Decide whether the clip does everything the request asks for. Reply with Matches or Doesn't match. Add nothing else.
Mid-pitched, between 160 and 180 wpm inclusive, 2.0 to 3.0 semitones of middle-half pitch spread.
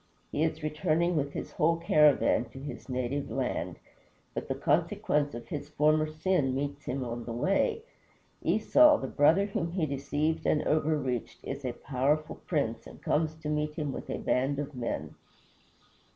Matches